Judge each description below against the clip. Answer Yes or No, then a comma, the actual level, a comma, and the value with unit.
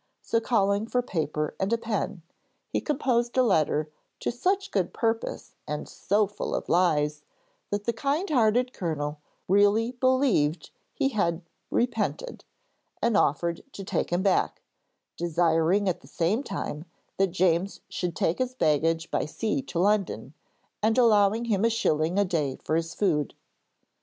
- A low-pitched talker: No, high, 195 Hz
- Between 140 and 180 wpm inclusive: Yes, average, 150 wpm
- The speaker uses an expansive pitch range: Yes, wide, 5.9 semitones